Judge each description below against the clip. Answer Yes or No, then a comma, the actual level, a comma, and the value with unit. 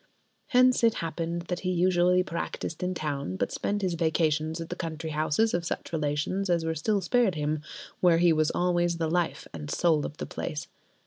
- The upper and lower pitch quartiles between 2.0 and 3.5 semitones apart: Yes, narrow, 2.5 semitones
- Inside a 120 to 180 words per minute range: No, average, 195 wpm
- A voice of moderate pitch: Yes, medium, 170 Hz